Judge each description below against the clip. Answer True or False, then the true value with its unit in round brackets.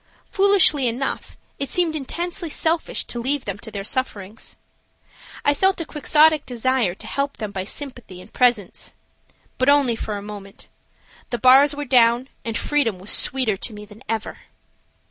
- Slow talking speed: False (165 wpm)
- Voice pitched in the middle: False (255 Hz)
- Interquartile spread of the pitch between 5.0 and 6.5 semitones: True (5.4 semitones)